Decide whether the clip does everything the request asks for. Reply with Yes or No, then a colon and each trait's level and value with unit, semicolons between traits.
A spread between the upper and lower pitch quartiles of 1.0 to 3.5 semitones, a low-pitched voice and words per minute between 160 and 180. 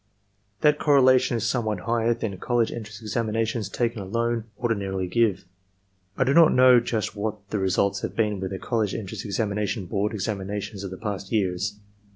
Yes: average, 2.9 semitones; low, 110 Hz; average, 170 wpm